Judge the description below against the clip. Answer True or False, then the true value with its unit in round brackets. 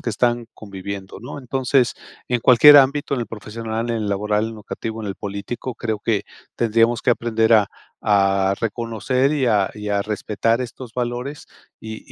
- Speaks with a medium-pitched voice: False (115 Hz)